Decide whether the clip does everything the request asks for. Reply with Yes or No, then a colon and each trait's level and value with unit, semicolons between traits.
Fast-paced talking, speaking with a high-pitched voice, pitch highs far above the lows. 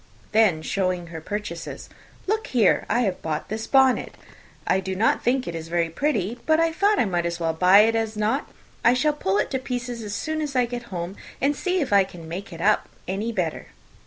Yes: fast, 220 wpm; high, 210 Hz; wide, 6.0 semitones